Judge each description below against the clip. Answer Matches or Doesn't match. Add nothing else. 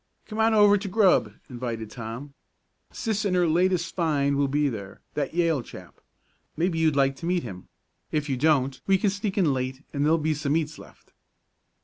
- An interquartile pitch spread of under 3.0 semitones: Doesn't match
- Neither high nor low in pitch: Matches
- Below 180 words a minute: Doesn't match